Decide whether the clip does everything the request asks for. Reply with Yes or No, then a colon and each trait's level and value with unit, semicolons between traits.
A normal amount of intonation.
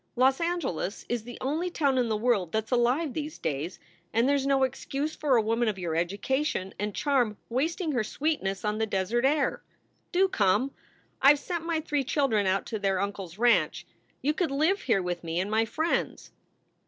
No: wide, 6.3 semitones